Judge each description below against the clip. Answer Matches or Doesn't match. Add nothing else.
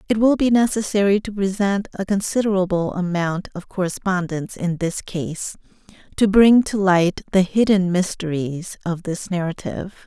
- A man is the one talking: Doesn't match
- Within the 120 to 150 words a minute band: Matches